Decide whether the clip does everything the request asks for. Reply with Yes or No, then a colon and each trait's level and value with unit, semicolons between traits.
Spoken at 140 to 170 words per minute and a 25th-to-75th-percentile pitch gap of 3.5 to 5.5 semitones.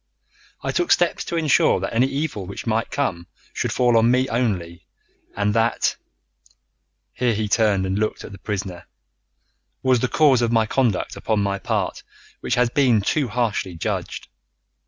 Yes: average, 160 wpm; average, 4.2 semitones